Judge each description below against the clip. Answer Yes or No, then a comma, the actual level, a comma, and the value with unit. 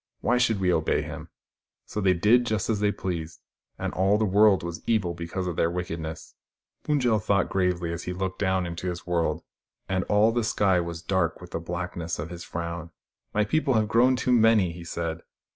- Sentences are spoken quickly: Yes, fast, 215 wpm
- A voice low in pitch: Yes, very low, 90 Hz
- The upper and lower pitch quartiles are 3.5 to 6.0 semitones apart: Yes, average, 3.8 semitones